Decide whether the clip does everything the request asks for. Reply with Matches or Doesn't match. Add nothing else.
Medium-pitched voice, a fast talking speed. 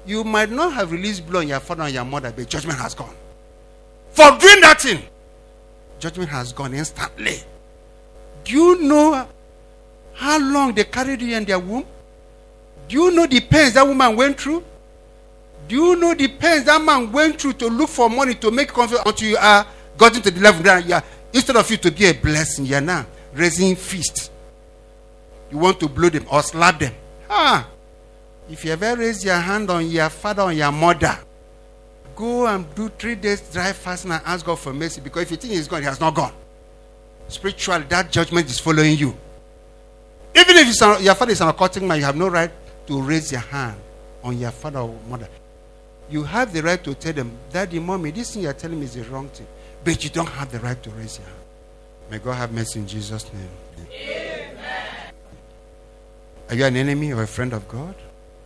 Matches